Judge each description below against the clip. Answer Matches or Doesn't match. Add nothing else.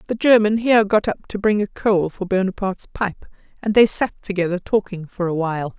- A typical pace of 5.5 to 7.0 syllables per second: Matches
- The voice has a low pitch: Doesn't match